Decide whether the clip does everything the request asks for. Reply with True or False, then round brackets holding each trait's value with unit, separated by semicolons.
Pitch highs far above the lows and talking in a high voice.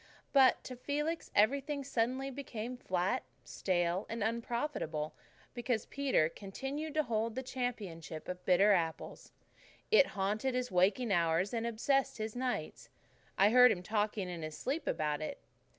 True (5.9 semitones; 225 Hz)